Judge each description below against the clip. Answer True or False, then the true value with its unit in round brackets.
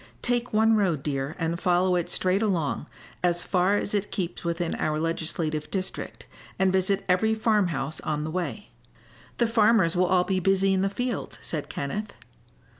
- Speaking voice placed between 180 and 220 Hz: True (185 Hz)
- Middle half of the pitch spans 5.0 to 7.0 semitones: False (3.6 semitones)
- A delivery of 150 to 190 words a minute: True (175 wpm)